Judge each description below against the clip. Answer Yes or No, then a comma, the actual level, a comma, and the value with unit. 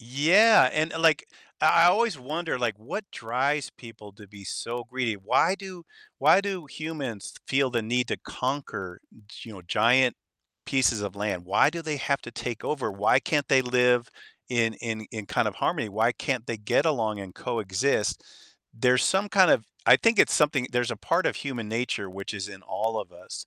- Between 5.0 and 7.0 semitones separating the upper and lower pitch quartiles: Yes, wide, 5.5 semitones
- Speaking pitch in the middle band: No, low, 125 Hz